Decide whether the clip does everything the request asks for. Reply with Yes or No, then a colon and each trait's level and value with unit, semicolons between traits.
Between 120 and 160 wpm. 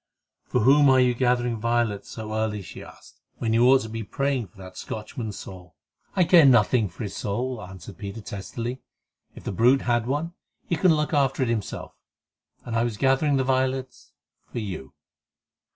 No: average, 180 wpm